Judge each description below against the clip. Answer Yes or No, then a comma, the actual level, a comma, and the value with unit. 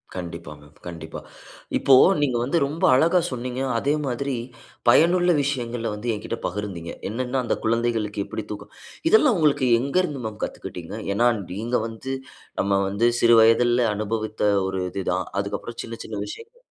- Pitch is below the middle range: Yes, low, 115 Hz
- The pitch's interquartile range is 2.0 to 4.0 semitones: No, average, 4.7 semitones